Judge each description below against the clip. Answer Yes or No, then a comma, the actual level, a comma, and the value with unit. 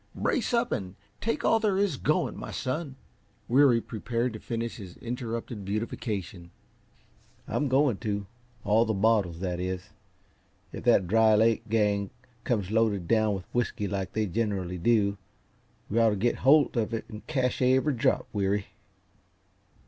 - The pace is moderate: Yes, average, 155 wpm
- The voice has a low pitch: Yes, low, 110 Hz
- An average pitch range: Yes, average, 3.4 semitones